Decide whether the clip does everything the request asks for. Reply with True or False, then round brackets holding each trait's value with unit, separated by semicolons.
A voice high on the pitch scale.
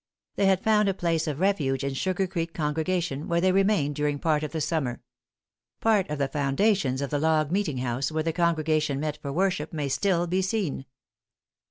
False (160 Hz)